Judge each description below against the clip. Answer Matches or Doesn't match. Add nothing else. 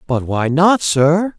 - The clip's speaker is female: Doesn't match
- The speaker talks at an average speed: Matches